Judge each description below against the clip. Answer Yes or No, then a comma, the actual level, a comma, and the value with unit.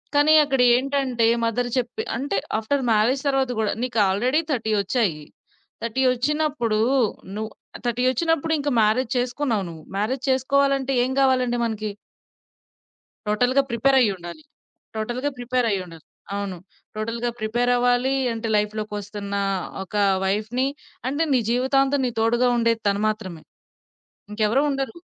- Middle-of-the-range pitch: No, high, 245 Hz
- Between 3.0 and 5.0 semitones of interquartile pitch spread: Yes, average, 3.6 semitones